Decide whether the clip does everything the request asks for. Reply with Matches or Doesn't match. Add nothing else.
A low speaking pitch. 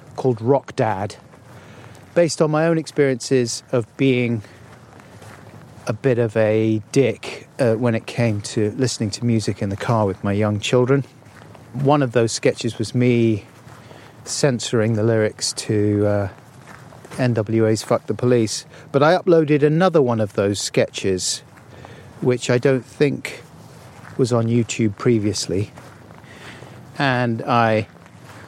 Matches